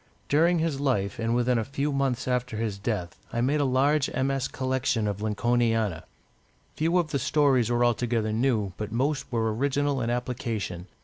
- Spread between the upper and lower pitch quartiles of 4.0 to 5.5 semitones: No, average, 3.6 semitones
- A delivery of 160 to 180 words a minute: Yes, average, 175 wpm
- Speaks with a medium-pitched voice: No, low, 125 Hz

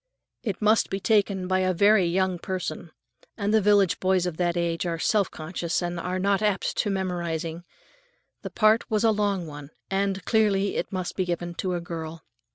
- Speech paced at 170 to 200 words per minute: Yes, average, 185 wpm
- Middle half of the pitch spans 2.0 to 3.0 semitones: Yes, average, 2.7 semitones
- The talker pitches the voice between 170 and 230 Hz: Yes, medium, 185 Hz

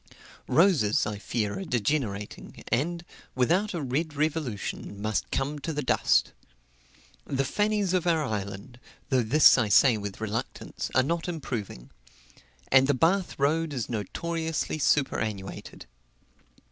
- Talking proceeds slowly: Yes, slow, 130 wpm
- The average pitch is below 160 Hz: Yes, low, 135 Hz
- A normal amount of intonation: No, wide, 7.0 semitones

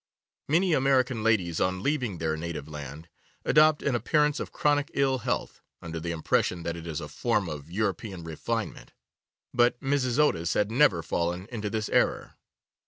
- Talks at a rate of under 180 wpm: Yes, average, 165 wpm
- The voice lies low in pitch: Yes, low, 105 Hz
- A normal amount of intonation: No, wide, 8.2 semitones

